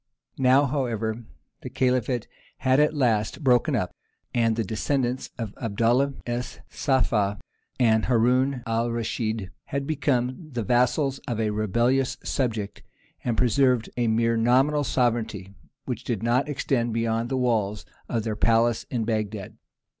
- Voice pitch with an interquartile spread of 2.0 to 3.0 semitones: Yes, narrow, 2.5 semitones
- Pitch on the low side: Yes, low, 120 Hz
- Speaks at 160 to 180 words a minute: No, average, 140 wpm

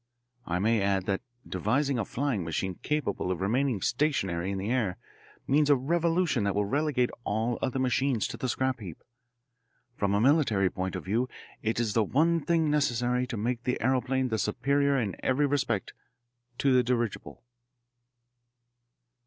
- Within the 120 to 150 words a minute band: No, average, 160 wpm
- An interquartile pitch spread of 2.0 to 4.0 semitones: No, wide, 5.5 semitones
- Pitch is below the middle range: Yes, low, 125 Hz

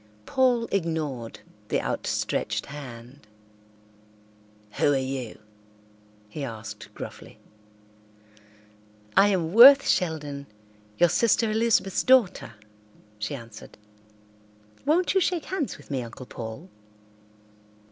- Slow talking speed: Yes, slow, 95 wpm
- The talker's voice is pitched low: No, medium, 155 Hz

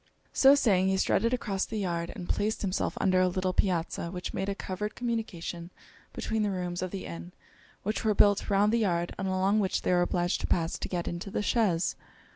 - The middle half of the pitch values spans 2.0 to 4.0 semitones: Yes, average, 2.9 semitones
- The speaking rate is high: Yes, fast, 215 wpm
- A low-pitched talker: No, high, 190 Hz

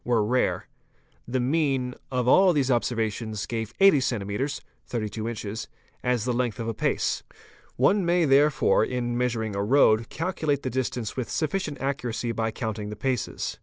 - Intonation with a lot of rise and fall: No, average, 3.5 semitones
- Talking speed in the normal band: Yes, average, 165 wpm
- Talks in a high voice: No, low, 125 Hz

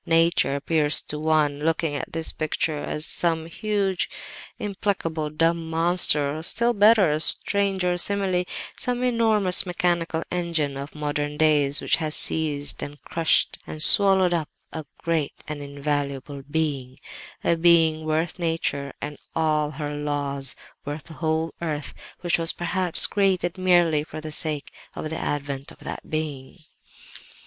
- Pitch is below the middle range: No, medium, 160 Hz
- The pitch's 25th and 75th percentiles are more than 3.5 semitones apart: No, average, 3.0 semitones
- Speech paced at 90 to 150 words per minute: Yes, average, 140 wpm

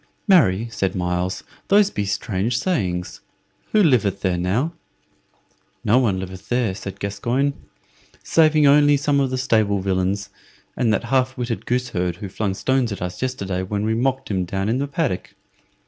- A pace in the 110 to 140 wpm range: No, average, 170 wpm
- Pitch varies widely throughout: Yes, wide, 5.7 semitones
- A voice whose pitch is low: Yes, low, 110 Hz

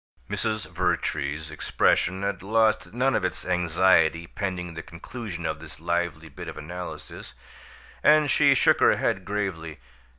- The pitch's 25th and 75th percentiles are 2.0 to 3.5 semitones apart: No, average, 4.0 semitones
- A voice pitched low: Yes, very low, 90 Hz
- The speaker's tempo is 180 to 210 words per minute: No, average, 140 wpm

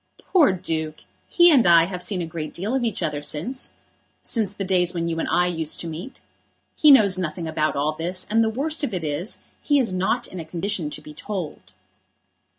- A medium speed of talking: No, fast, 215 wpm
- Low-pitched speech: No, medium, 180 Hz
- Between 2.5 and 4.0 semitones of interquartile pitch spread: No, average, 5.0 semitones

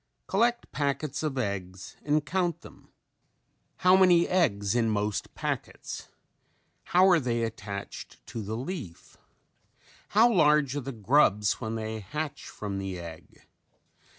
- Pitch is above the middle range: No, low, 130 Hz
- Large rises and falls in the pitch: Yes, wide, 7.8 semitones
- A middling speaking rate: No, slow, 130 wpm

